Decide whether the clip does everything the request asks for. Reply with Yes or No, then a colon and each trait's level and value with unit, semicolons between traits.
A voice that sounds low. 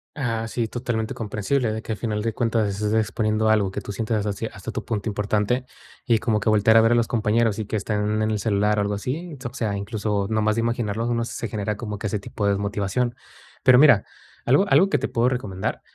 Yes: low, 110 Hz